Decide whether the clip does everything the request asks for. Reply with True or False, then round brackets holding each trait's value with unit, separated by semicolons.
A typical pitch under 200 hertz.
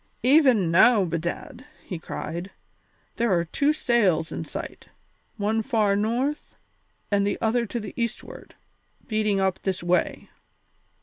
False (210 Hz)